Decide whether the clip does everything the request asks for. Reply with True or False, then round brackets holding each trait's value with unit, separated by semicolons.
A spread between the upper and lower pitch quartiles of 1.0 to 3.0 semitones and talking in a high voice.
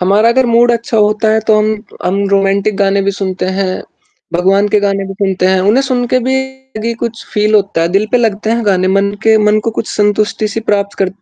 True (2.5 semitones; 210 Hz)